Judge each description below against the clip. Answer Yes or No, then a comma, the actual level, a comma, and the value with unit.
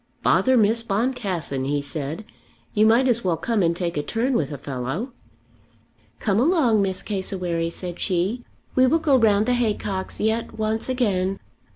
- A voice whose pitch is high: Yes, high, 205 Hz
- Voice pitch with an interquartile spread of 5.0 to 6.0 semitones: Yes, wide, 5.4 semitones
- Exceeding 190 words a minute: No, average, 165 wpm